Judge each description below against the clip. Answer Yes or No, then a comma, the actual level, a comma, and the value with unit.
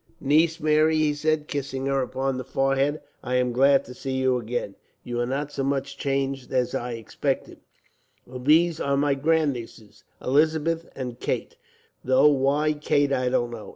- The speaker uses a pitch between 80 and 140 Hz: Yes, low, 135 Hz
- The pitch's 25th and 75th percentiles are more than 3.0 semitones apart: No, average, 2.7 semitones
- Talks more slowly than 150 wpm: No, average, 170 wpm